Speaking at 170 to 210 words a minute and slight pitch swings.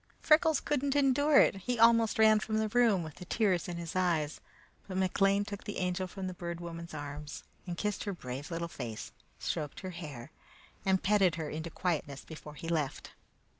No: average, 195 wpm; average, 4.6 semitones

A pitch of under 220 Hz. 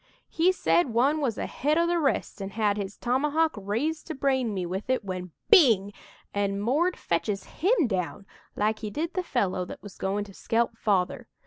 No: high, 225 Hz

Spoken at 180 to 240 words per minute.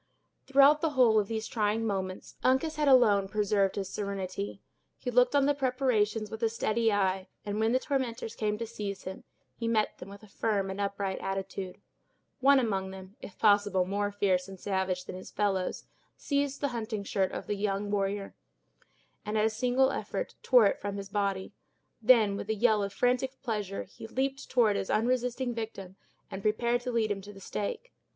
Yes: average, 190 wpm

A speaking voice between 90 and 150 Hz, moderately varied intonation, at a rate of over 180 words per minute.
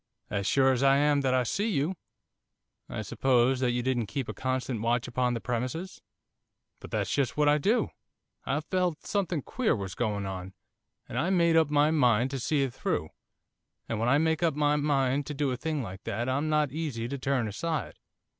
Yes: low, 135 Hz; average, 3.8 semitones; fast, 205 wpm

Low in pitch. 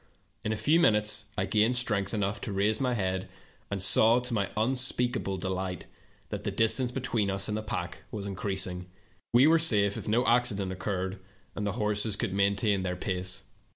Yes: low, 105 Hz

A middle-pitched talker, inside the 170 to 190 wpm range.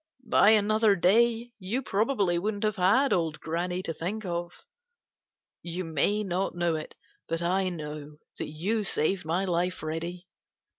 No: medium, 180 Hz; average, 150 wpm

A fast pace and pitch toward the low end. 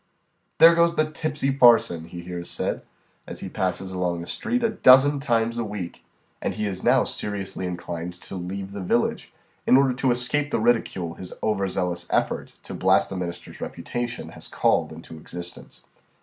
No: average, 180 wpm; low, 100 Hz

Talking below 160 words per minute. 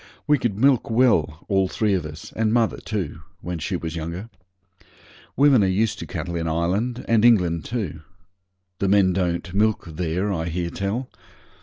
No: average, 170 wpm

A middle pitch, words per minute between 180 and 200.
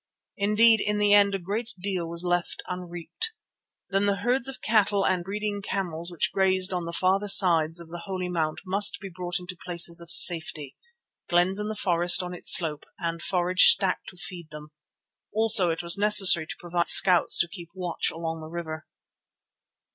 Yes: medium, 180 Hz; average, 185 wpm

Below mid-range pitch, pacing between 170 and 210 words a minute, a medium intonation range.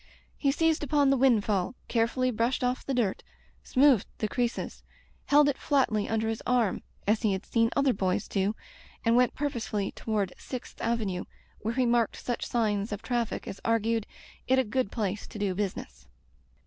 No: high, 230 Hz; average, 175 wpm; average, 3.5 semitones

